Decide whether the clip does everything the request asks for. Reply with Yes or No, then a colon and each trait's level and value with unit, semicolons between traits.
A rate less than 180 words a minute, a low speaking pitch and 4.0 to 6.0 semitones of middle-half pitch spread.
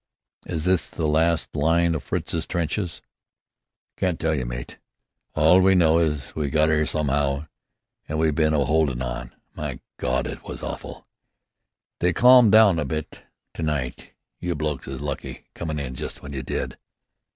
No: average, 165 wpm; very low, 80 Hz; average, 2.8 semitones